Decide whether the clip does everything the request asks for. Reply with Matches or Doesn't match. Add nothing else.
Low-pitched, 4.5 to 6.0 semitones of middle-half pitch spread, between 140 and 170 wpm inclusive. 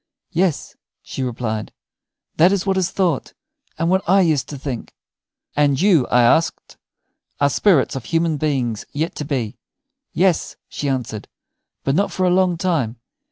Doesn't match